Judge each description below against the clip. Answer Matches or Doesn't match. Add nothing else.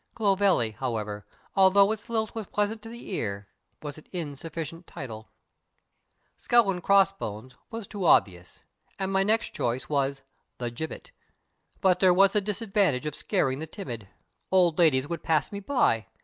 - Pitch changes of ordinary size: Doesn't match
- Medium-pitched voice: Matches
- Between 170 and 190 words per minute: Doesn't match